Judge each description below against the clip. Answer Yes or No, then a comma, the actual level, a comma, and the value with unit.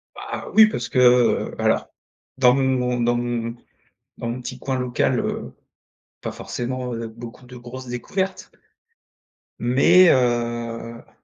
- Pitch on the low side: Yes, low, 125 Hz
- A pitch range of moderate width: No, narrow, 1.5 semitones